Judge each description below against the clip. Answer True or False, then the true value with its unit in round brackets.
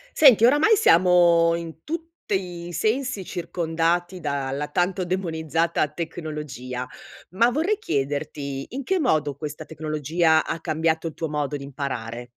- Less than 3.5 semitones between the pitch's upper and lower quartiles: False (3.8 semitones)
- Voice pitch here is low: False (165 Hz)